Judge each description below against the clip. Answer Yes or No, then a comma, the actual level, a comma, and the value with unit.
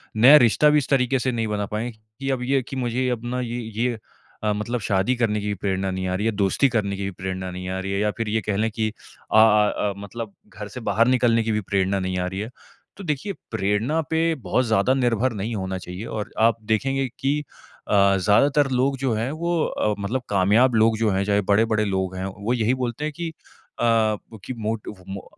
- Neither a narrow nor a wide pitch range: Yes, average, 3.9 semitones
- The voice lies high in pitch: No, low, 110 Hz